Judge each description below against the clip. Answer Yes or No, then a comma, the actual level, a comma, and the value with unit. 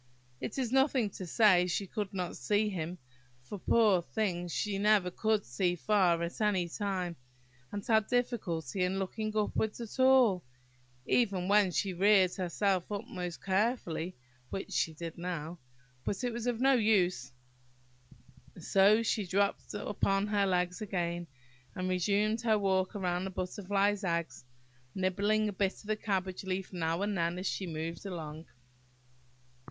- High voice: Yes, high, 195 Hz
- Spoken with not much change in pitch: No, average, 3.0 semitones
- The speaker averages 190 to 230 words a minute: No, average, 155 wpm